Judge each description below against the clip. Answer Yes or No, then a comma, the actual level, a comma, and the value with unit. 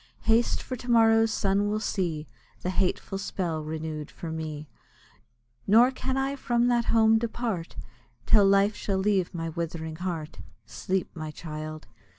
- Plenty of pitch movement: Yes, wide, 5.8 semitones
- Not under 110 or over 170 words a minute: Yes, average, 150 wpm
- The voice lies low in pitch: No, high, 195 Hz